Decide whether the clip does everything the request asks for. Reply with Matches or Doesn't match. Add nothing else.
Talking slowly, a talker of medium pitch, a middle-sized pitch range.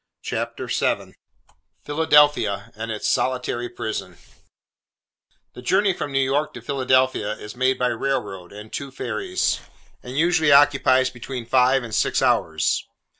Doesn't match